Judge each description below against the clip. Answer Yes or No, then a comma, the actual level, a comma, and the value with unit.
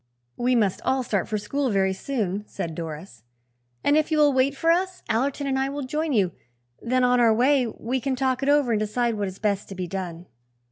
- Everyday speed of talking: No, fast, 225 wpm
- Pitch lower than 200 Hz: No, high, 245 Hz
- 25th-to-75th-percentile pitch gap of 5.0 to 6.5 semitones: Yes, wide, 5.4 semitones